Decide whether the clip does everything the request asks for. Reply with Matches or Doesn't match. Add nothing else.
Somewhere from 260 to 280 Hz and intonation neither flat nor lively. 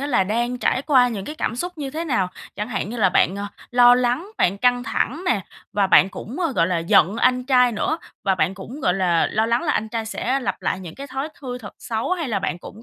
Doesn't match